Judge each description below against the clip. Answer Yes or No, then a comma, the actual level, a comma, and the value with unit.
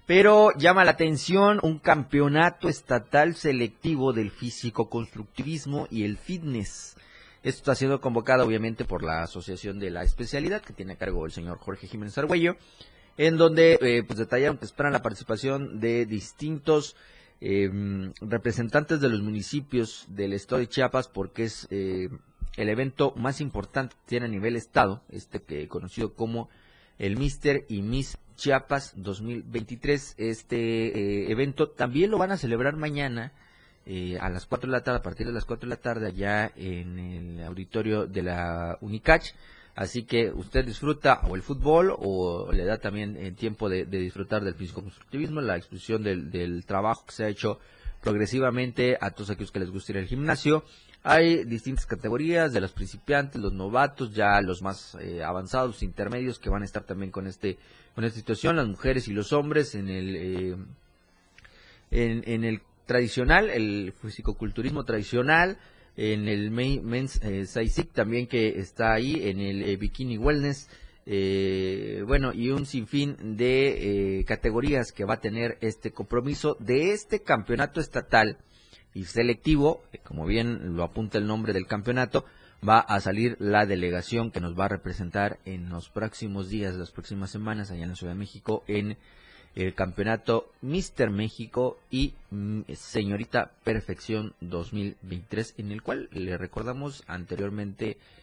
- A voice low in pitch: Yes, low, 110 Hz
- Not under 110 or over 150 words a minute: No, average, 160 wpm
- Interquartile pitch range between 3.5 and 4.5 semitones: No, average, 4.9 semitones